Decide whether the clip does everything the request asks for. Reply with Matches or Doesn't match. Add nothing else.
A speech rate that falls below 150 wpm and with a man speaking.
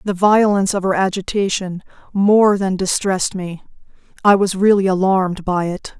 Doesn't match